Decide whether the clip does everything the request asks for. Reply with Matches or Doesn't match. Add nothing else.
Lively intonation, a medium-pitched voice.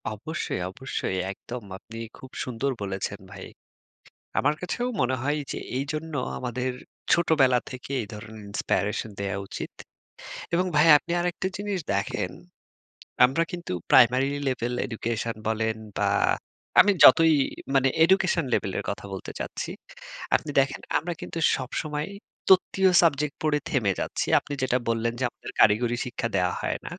Doesn't match